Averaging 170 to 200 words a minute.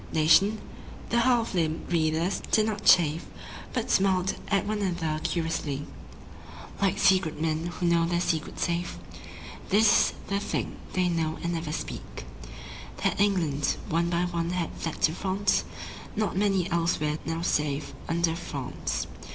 No: average, 145 wpm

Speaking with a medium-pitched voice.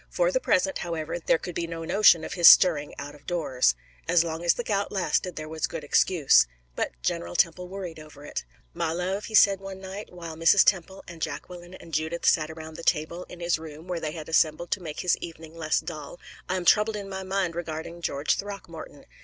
Yes: medium, 170 Hz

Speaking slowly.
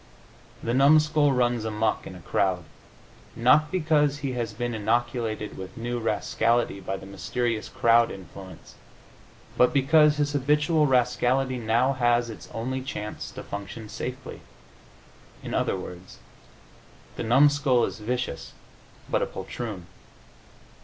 Yes: slow, 125 wpm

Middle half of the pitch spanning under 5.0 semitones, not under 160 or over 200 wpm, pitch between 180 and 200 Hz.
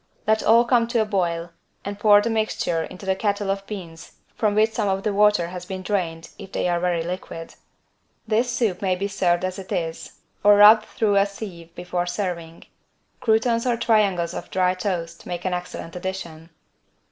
Yes: average, 3.2 semitones; average, 190 wpm; high, 190 Hz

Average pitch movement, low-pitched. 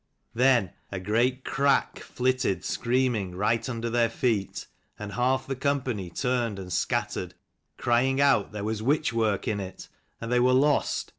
Yes: average, 3.8 semitones; low, 120 Hz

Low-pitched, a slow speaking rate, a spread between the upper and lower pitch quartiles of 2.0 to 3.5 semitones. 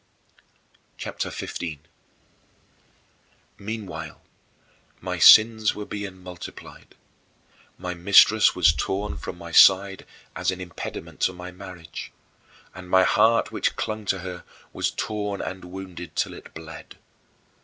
Yes: very low, 95 Hz; slow, 125 wpm; narrow, 2.5 semitones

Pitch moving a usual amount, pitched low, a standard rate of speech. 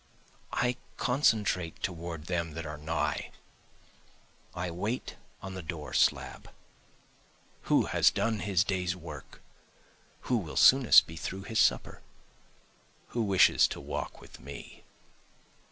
No: average, 4.1 semitones; very low, 90 Hz; slow, 125 wpm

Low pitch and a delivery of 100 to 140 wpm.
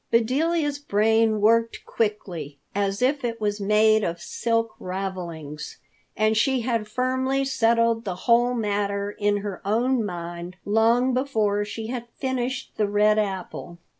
No: high, 220 Hz; slow, 135 wpm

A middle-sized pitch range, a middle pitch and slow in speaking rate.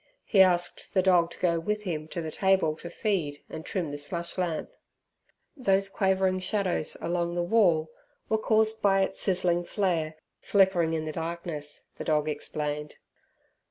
No: average, 3.3 semitones; medium, 175 Hz; average, 160 wpm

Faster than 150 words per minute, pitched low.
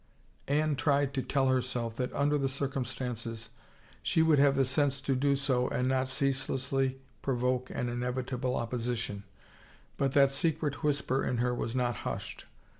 Yes: average, 160 wpm; low, 130 Hz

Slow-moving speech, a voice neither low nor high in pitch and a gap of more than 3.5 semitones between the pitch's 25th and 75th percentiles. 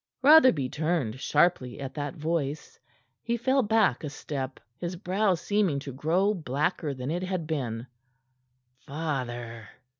Yes: slow, 130 wpm; medium, 155 Hz; wide, 5.5 semitones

